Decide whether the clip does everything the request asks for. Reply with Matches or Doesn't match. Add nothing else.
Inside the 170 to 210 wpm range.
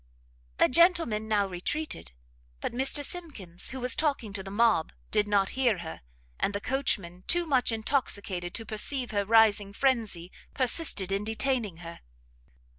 Doesn't match